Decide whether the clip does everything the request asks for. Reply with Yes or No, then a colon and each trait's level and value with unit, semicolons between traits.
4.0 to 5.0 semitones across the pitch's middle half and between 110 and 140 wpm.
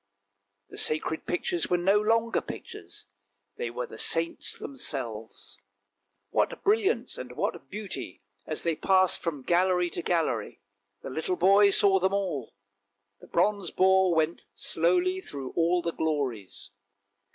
Yes: average, 4.4 semitones; slow, 135 wpm